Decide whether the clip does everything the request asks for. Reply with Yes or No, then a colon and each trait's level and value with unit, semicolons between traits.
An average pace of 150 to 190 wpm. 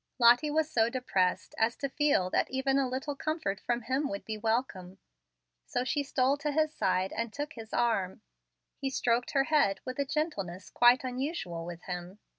Yes: average, 185 wpm